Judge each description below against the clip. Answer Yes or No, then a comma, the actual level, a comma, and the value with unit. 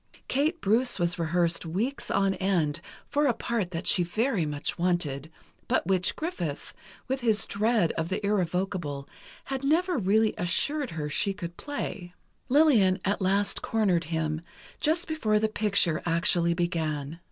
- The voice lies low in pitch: No, high, 190 Hz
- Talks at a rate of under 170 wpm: Yes, average, 150 wpm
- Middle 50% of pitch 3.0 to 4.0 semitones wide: No, average, 5.2 semitones